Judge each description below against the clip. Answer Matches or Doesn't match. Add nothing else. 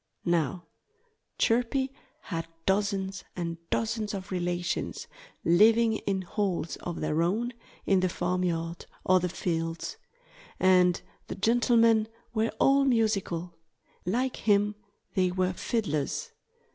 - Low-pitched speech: Doesn't match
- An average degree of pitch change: Matches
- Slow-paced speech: Matches